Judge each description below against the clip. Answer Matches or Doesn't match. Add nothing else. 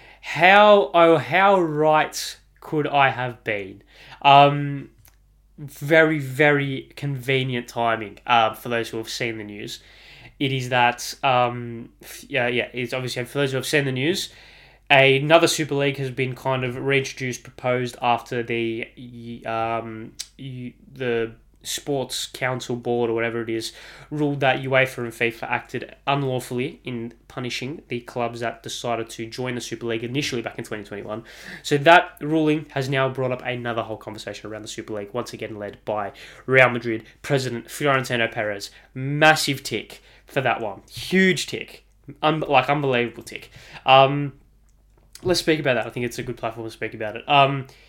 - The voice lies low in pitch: Matches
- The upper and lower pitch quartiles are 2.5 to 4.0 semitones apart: Matches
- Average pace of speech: Matches